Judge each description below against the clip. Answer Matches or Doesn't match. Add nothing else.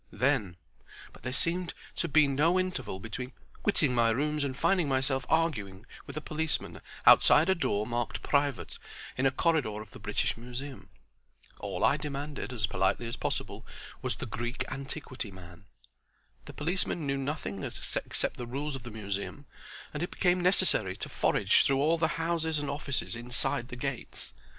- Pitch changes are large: Doesn't match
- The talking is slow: Doesn't match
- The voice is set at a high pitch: Doesn't match